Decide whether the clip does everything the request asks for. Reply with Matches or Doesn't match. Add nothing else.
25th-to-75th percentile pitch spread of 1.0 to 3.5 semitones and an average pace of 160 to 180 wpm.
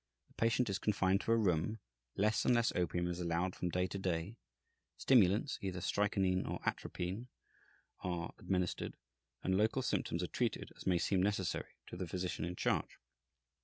Matches